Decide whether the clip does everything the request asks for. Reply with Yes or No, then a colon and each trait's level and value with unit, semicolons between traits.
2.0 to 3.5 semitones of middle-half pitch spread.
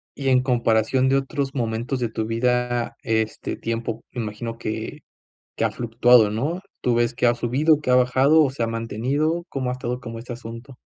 Yes: narrow, 2.5 semitones